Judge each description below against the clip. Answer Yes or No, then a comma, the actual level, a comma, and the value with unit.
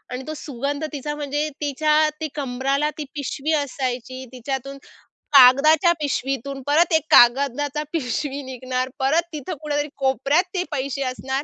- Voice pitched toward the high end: Yes, very high, 280 Hz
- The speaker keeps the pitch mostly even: Yes, narrow, 2.3 semitones